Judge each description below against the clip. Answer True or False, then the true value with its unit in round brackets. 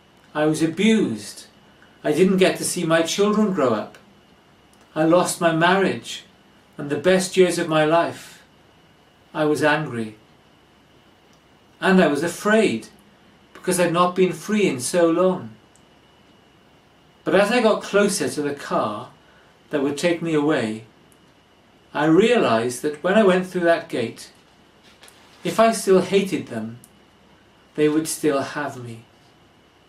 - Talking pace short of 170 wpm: True (140 wpm)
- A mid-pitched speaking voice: True (165 Hz)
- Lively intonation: False (3.9 semitones)